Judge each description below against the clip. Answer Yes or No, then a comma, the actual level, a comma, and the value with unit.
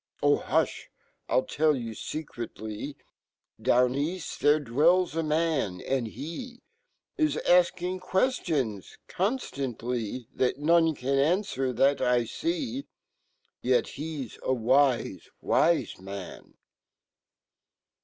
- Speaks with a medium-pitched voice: Yes, medium, 145 Hz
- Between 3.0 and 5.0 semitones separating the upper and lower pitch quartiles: No, wide, 5.6 semitones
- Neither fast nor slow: No, slow, 100 wpm